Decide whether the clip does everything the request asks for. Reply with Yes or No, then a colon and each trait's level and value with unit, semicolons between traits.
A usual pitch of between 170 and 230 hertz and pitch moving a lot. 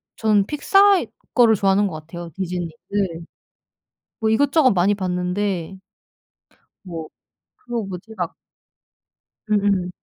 No: high, 195 Hz; average, 3.7 semitones